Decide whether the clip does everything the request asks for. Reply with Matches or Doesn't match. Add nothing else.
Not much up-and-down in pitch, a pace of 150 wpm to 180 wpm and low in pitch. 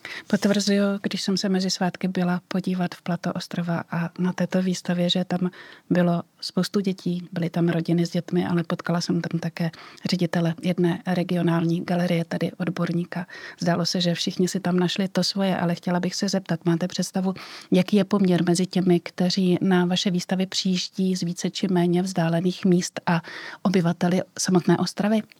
Doesn't match